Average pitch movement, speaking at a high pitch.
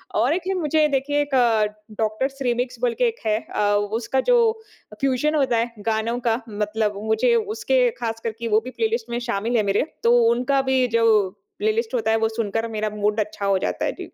Yes: average, 3.5 semitones; high, 235 Hz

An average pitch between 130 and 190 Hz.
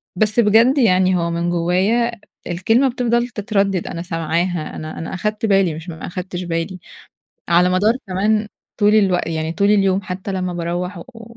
Yes: medium, 185 Hz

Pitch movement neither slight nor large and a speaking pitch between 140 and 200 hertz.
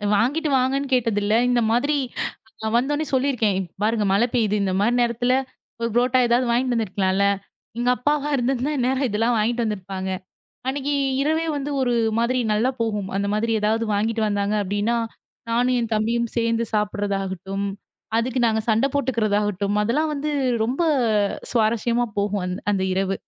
No: average, 3.5 semitones; high, 230 Hz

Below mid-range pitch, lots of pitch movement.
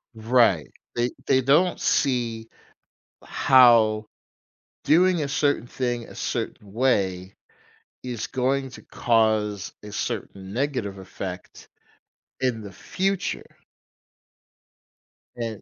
No: low, 120 Hz; average, 4.0 semitones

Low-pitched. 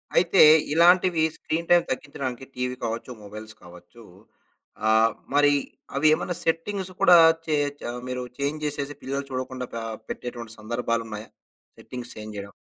Yes: low, 130 Hz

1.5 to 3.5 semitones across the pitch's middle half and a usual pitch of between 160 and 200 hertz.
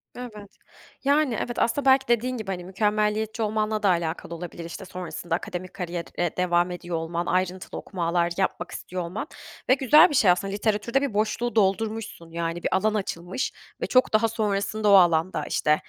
No: average, 4.0 semitones; high, 195 Hz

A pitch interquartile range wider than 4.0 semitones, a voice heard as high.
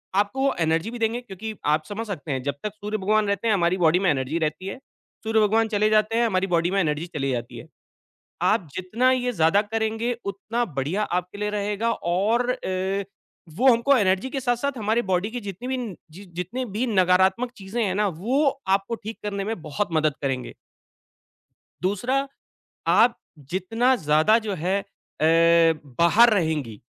Yes: average, 4.4 semitones; high, 205 Hz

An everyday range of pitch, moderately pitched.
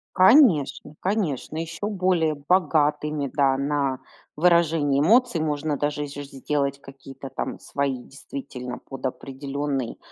Yes: average, 3.0 semitones; medium, 145 Hz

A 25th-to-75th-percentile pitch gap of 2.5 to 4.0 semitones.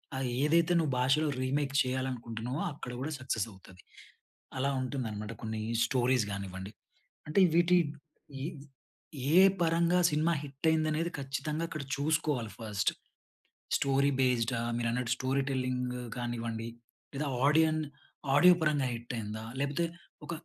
No: average, 4.4 semitones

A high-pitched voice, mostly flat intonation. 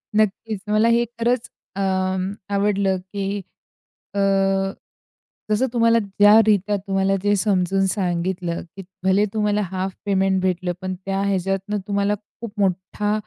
Yes: high, 195 Hz; narrow, 1.8 semitones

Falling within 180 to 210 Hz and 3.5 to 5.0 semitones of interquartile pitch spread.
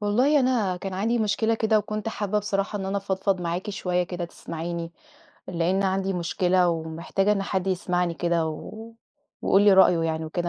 No: high, 190 Hz; average, 3.0 semitones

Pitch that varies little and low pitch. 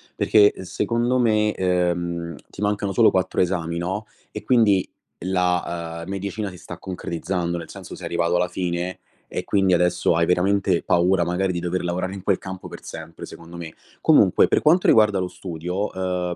Yes: narrow, 2.2 semitones; very low, 90 Hz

